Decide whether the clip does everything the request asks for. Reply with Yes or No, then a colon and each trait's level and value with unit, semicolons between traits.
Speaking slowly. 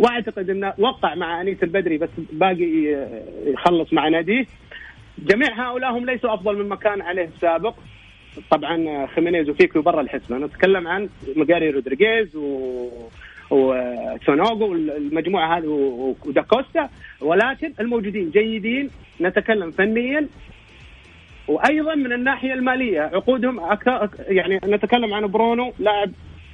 Yes: slow, 120 wpm